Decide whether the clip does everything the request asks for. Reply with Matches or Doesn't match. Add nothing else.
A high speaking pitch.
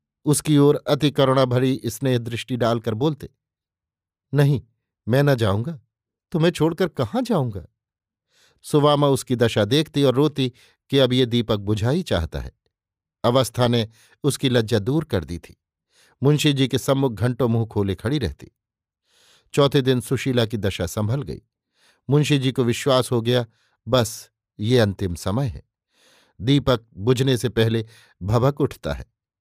Doesn't match